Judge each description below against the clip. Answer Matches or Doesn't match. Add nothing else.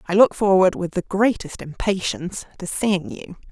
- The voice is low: Doesn't match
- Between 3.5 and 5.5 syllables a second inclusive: Matches